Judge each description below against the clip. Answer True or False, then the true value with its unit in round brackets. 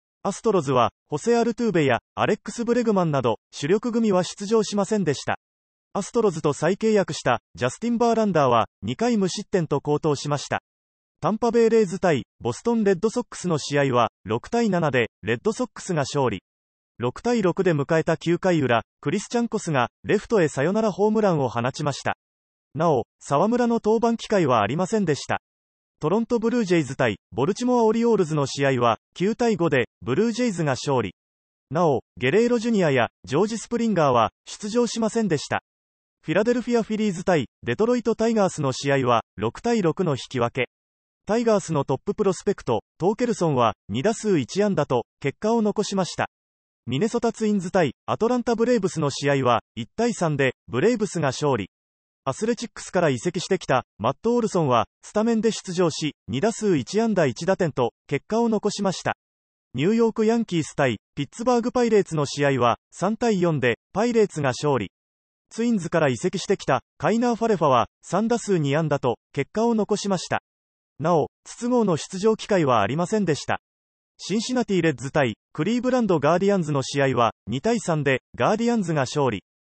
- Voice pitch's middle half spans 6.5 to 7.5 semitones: False (8.8 semitones)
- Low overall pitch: False (175 Hz)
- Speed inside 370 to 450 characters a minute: True (385 characters per minute)